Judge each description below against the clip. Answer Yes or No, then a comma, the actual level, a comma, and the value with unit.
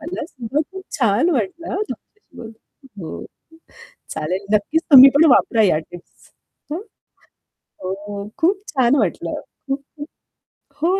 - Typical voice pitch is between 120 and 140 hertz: No, very high, 255 Hz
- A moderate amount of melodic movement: No, wide, 8.4 semitones